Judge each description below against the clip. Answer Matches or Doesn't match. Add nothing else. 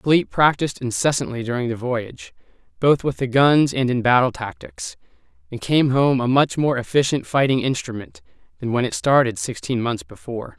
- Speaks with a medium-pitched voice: Doesn't match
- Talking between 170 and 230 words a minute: Matches